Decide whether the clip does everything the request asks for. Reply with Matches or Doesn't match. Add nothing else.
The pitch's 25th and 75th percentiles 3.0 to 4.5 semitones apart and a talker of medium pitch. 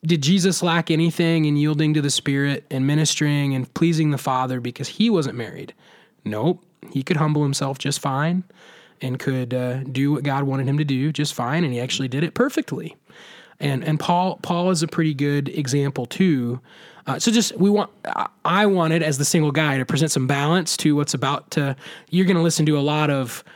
Matches